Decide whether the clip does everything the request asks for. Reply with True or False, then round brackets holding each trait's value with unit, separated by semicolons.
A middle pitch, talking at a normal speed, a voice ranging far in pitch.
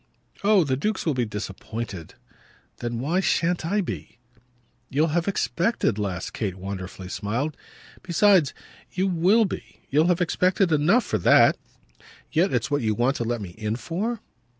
True (150 Hz; 155 wpm; 8.6 semitones)